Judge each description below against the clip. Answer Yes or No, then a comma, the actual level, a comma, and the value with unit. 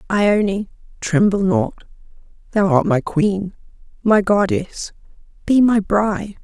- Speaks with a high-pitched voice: Yes, high, 205 Hz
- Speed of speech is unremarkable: No, slow, 95 wpm